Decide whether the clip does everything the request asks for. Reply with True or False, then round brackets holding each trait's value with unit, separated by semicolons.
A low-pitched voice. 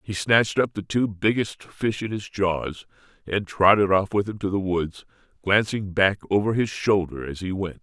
True (100 Hz)